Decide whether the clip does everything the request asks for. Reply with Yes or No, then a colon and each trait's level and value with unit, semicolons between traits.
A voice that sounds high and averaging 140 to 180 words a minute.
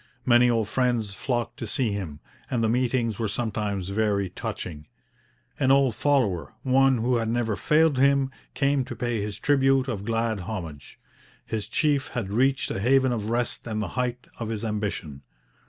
No: low, 115 Hz; average, 170 wpm